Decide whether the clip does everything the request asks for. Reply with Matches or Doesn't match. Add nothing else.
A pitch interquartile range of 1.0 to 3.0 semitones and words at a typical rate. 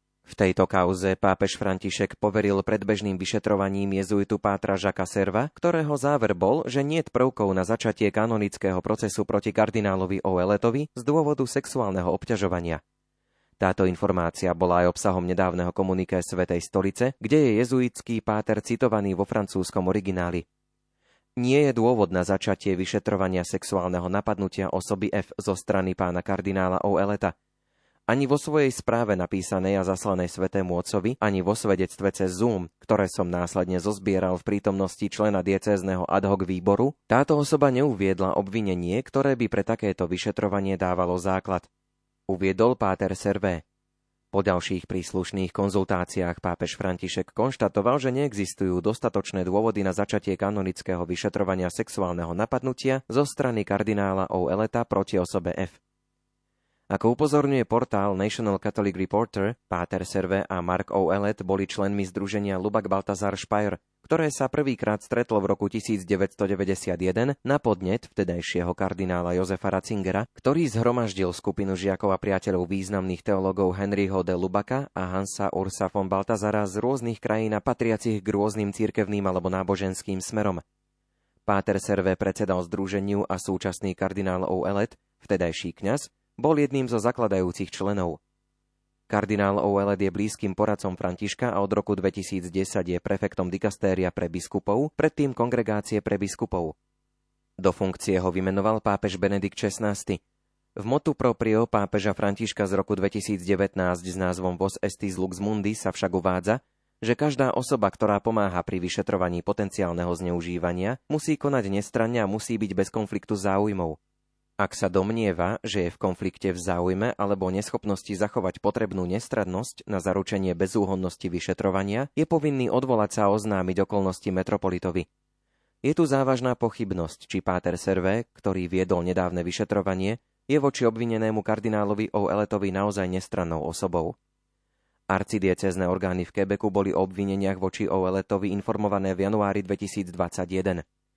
Matches